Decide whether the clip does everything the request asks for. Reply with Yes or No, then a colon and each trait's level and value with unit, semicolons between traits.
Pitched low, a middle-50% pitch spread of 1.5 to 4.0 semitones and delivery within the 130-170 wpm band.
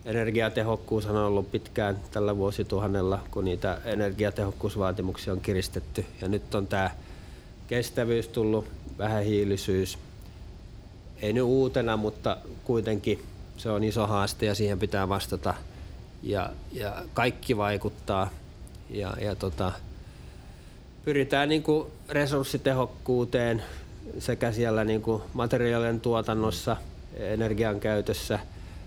No: low, 105 Hz; average, 2.9 semitones; average, 100 wpm